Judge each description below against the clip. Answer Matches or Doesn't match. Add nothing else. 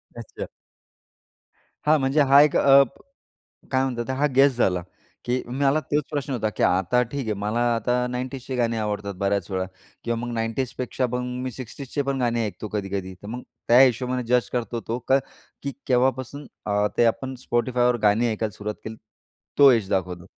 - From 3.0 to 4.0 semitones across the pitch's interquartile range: Matches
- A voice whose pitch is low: Matches